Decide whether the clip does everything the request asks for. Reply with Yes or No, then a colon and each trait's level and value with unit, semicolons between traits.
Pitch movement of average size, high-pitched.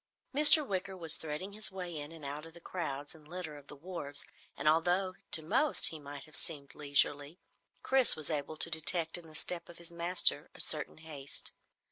No: average, 3.3 semitones; medium, 160 Hz